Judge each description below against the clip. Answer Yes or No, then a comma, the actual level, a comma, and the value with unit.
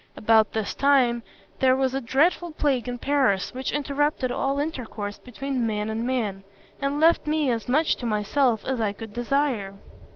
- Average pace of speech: Yes, average, 170 wpm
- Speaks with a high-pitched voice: Yes, very high, 255 Hz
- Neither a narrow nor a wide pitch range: Yes, average, 4.0 semitones